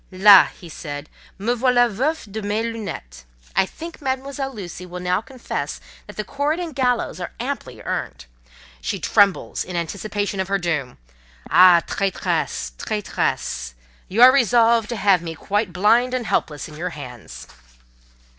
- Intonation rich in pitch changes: Yes, wide, 5.8 semitones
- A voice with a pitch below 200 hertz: No, high, 205 Hz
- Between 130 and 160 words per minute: Yes, average, 155 wpm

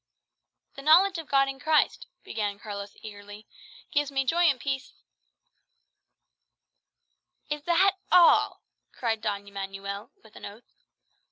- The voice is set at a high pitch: Yes, very high, 260 Hz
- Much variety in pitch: Yes, wide, 6.7 semitones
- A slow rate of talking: Yes, slow, 125 wpm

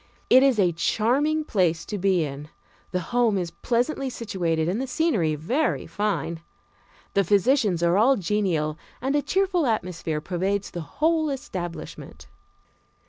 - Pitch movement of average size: No, wide, 7.3 semitones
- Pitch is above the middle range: Yes, high, 200 Hz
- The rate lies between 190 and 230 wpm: No, average, 140 wpm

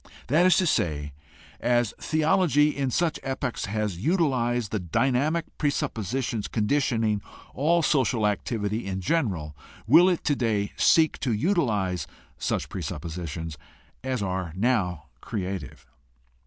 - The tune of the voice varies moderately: No, wide, 7.2 semitones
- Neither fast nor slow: No, slow, 120 wpm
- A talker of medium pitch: No, low, 120 Hz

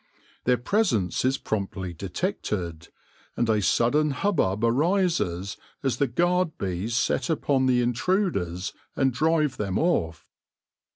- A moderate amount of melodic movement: No, wide, 8.2 semitones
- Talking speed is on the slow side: Yes, slow, 120 wpm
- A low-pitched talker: Yes, low, 120 Hz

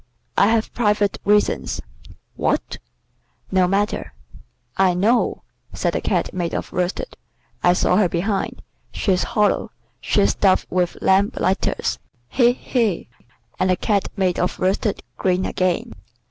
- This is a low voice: No, high, 190 Hz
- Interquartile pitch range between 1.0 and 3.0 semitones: Yes, narrow, 2.4 semitones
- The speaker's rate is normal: No, slow, 130 wpm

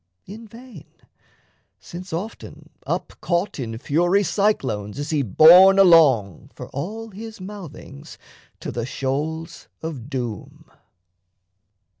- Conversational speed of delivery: No, slow, 110 wpm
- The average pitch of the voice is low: No, medium, 165 Hz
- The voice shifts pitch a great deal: Yes, wide, 6.6 semitones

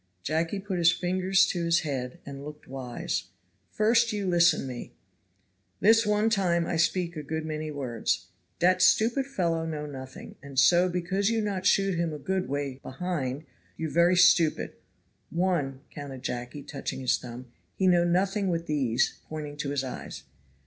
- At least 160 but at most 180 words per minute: Yes, average, 165 wpm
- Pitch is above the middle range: No, medium, 165 Hz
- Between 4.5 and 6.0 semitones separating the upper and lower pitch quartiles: Yes, average, 4.8 semitones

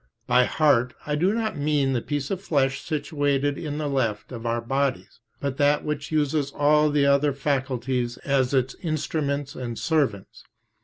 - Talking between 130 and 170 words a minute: Yes, average, 165 wpm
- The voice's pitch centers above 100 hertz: Yes, medium, 140 Hz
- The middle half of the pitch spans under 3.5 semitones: Yes, narrow, 2.4 semitones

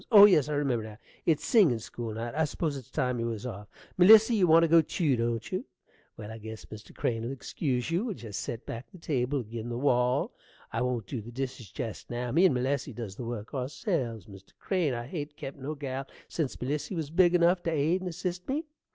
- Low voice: Yes, low, 130 Hz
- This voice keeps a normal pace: No, fast, 225 wpm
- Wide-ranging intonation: Yes, wide, 5.9 semitones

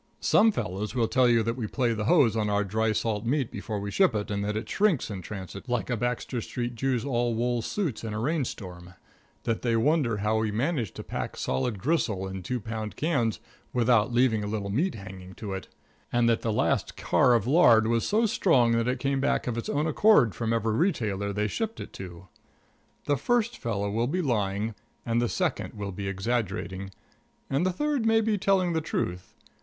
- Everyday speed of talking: No, fast, 210 wpm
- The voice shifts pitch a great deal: No, average, 4.6 semitones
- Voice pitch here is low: Yes, low, 115 Hz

